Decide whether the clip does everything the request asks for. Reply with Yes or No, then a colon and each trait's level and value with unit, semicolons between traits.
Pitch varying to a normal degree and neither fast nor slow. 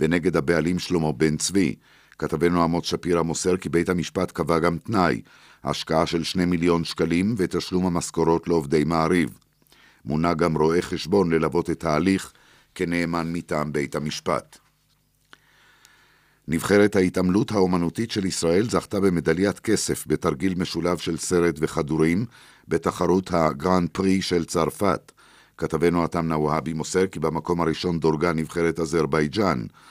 No: narrow, 2.0 semitones; average, 125 wpm